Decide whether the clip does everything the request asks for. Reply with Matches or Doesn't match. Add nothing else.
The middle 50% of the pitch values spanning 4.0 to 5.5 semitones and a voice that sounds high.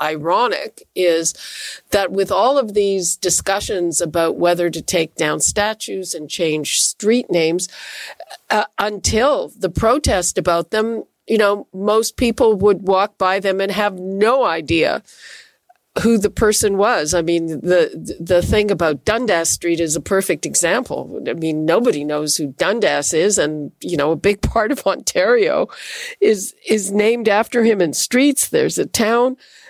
Matches